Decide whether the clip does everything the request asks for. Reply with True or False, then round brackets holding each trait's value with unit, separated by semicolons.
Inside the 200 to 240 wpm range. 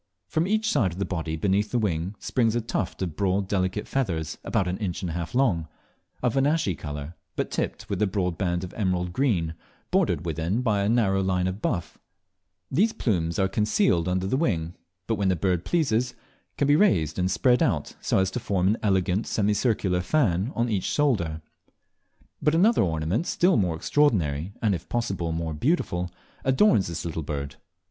False (190 wpm)